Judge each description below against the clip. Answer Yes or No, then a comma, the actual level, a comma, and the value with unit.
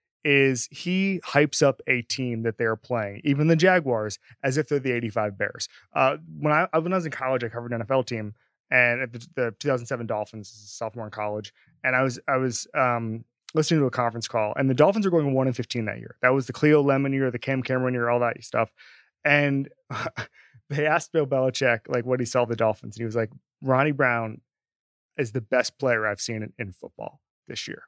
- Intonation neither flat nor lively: Yes, average, 3.3 semitones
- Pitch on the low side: Yes, low, 125 Hz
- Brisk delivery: Yes, fast, 220 wpm